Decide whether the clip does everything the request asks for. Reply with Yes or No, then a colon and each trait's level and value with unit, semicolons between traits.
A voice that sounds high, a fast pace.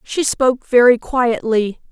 No: high, 245 Hz; slow, 125 wpm